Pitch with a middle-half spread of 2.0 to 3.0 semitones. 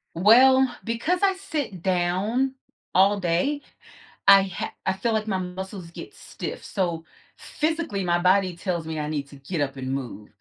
No: wide, 5.4 semitones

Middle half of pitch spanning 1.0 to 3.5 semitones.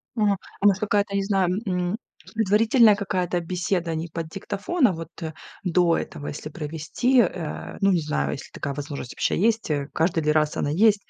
No: average, 4.2 semitones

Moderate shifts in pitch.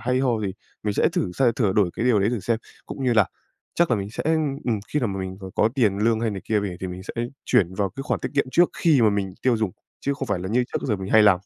Yes: average, 4.1 semitones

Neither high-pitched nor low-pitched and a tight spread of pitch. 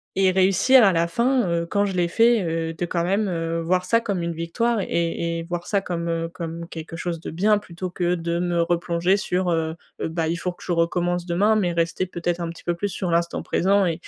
Yes: medium, 175 Hz; narrow, 2.1 semitones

